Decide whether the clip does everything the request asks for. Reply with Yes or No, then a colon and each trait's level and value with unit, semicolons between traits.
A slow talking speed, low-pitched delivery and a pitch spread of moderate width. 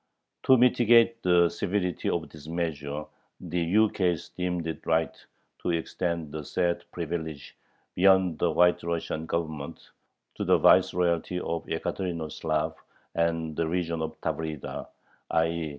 No: slow, 130 wpm; very low, 85 Hz; narrow, 2.0 semitones